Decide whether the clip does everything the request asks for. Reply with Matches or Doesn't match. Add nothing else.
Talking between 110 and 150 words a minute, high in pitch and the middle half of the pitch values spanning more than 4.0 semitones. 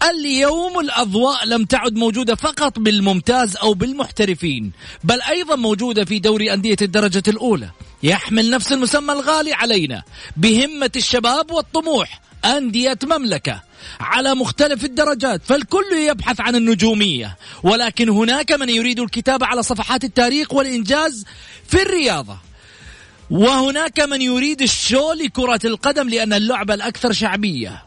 Matches